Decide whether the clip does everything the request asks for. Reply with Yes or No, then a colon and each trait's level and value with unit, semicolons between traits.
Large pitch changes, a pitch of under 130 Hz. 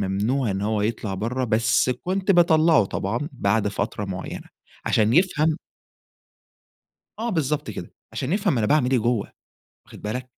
Yes: wide, 6.5 semitones; low, 120 Hz